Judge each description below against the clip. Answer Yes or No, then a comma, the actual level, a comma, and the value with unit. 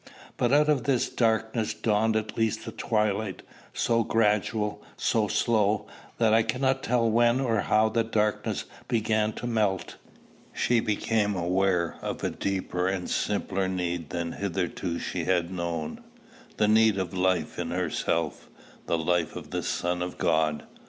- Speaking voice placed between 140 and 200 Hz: No, low, 105 Hz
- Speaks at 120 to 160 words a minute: Yes, average, 150 wpm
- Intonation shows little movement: No, average, 4.0 semitones